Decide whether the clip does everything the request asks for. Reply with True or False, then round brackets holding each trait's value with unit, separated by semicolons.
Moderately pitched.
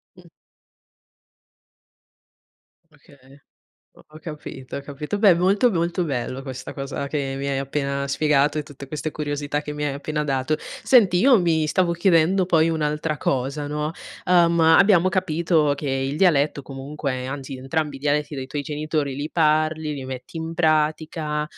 True (150 Hz)